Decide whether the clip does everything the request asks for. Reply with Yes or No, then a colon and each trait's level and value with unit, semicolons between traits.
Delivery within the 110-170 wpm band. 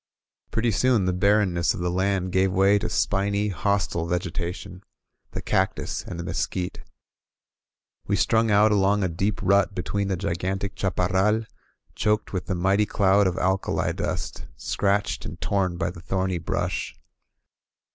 Yes: average, 150 wpm